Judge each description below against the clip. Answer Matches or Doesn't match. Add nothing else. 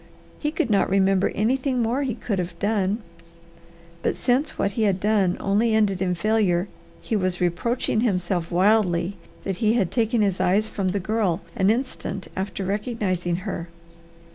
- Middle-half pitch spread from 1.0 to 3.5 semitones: Matches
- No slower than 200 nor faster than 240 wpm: Doesn't match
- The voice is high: Matches